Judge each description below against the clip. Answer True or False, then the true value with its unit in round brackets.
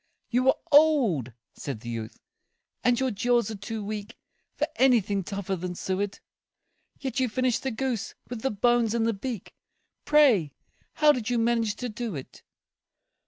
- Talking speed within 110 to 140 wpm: False (165 wpm)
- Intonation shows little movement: False (4.1 semitones)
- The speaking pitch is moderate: False (230 Hz)